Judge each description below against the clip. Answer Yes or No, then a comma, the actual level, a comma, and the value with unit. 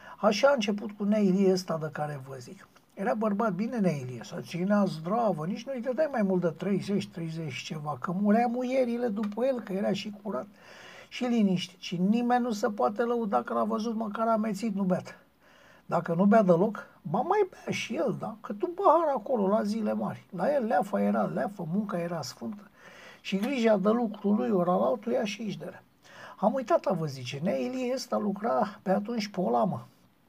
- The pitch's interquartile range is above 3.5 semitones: Yes, average, 4.4 semitones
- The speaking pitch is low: No, high, 210 Hz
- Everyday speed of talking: No, fast, 190 wpm